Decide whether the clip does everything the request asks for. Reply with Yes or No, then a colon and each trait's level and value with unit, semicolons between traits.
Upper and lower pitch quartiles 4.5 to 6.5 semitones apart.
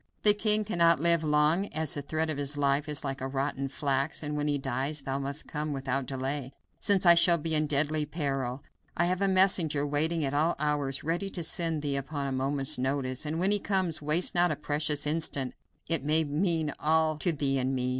No: average, 3.0 semitones